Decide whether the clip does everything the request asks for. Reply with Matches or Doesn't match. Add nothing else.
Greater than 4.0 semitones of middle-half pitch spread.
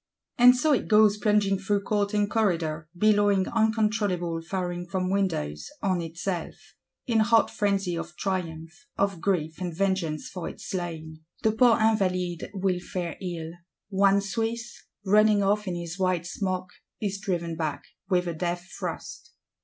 Doesn't match